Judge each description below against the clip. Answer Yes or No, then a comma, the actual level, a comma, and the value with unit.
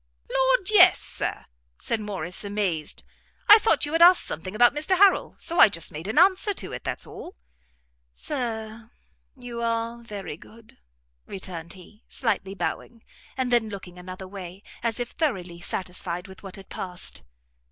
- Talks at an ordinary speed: Yes, average, 160 wpm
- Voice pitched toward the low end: No, high, 215 Hz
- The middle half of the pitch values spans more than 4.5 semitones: Yes, average, 5.1 semitones